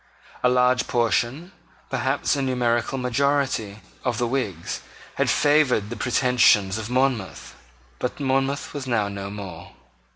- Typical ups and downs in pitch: Yes, average, 3.9 semitones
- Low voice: Yes, low, 125 Hz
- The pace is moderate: No, slow, 130 wpm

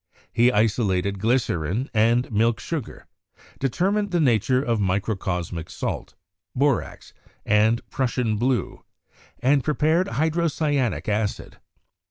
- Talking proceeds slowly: Yes, slow, 100 wpm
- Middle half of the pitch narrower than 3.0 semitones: No, average, 5.0 semitones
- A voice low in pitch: Yes, low, 120 Hz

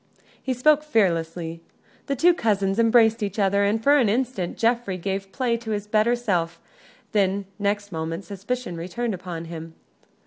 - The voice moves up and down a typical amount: Yes, average, 4.6 semitones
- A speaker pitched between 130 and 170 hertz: No, high, 205 Hz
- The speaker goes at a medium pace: Yes, average, 160 wpm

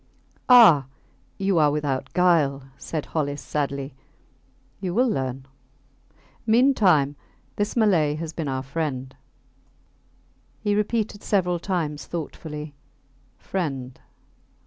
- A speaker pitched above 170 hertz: No, medium, 155 Hz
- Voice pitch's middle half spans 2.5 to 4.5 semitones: No, wide, 5.5 semitones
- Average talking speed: No, slow, 100 wpm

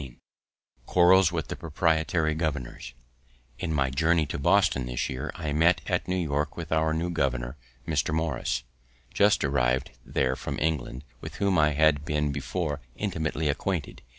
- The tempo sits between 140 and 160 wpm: Yes, average, 155 wpm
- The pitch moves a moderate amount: Yes, average, 3.0 semitones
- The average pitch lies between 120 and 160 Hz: No, very low, 80 Hz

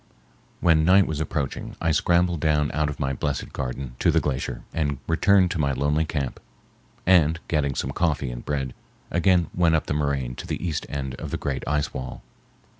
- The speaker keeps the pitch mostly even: No, average, 3.2 semitones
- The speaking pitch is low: Yes, very low, 75 Hz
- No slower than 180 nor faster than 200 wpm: Yes, average, 190 wpm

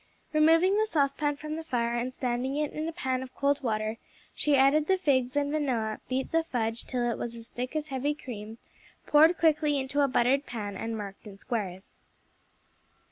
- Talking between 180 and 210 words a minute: Yes, average, 190 wpm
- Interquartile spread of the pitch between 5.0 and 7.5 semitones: No, average, 4.3 semitones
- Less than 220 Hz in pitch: No, very high, 265 Hz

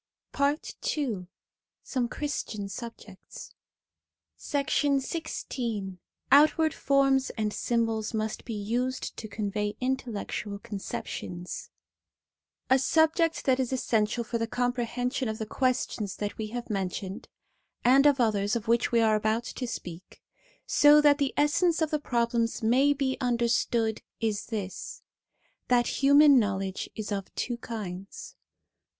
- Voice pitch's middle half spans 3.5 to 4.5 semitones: Yes, average, 4.0 semitones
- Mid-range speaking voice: No, high, 235 Hz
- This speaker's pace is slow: Yes, slow, 130 wpm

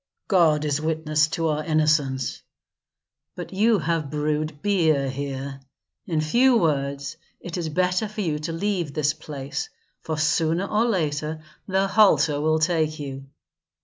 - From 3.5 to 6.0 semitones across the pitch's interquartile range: No, average, 3.0 semitones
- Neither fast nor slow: Yes, average, 145 wpm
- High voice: No, medium, 155 Hz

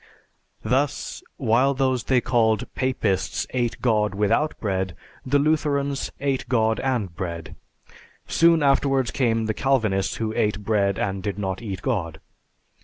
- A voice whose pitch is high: No, low, 115 Hz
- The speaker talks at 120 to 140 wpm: Yes, slow, 135 wpm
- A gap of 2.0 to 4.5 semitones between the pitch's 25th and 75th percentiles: No, average, 5.1 semitones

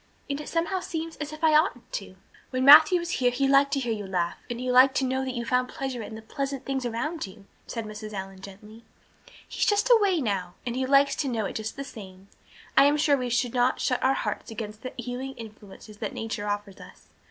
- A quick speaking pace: Yes, fast, 240 wpm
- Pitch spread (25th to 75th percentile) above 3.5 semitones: Yes, average, 4.5 semitones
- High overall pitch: Yes, very high, 250 Hz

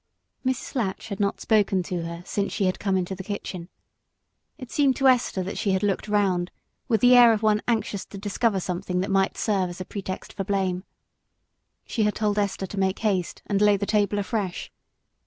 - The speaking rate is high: Yes, fast, 210 wpm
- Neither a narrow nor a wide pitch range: No, narrow, 2.2 semitones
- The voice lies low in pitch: No, high, 200 Hz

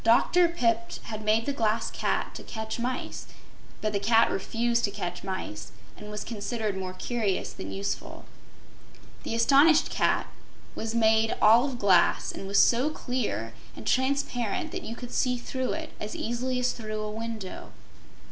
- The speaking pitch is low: No, high, 225 Hz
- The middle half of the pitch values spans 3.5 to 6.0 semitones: No, average, 2.8 semitones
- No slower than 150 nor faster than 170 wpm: Yes, average, 165 wpm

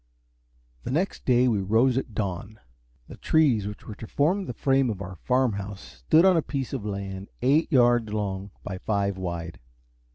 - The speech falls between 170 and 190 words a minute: Yes, average, 185 wpm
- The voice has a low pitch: Yes, low, 110 Hz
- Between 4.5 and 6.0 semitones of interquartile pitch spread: Yes, average, 5.1 semitones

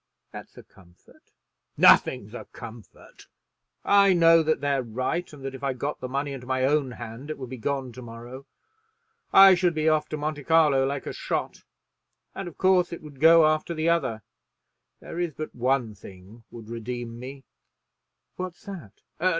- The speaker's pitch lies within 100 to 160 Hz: Yes, low, 135 Hz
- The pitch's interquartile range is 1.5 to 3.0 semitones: No, average, 4.5 semitones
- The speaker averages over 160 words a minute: Yes, average, 175 wpm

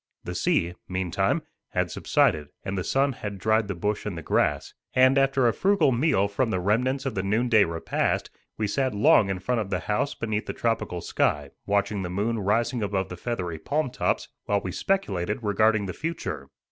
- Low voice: Yes, low, 105 Hz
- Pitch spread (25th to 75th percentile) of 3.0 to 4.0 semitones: No, average, 4.4 semitones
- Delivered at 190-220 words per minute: Yes, average, 195 wpm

